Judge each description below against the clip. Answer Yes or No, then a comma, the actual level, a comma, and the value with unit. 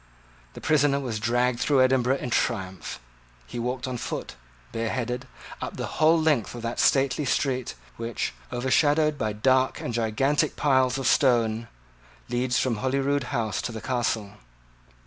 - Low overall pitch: Yes, low, 125 Hz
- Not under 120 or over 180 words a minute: Yes, average, 145 wpm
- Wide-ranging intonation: No, narrow, 2.6 semitones